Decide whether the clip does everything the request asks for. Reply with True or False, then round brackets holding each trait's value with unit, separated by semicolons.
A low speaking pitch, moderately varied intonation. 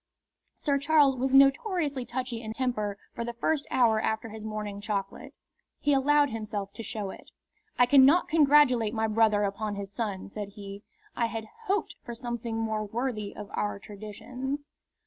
False (230 Hz; 4.2 semitones)